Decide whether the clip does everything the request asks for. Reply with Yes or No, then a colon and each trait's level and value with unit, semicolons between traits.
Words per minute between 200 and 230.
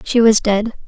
Yes: fast, 205 wpm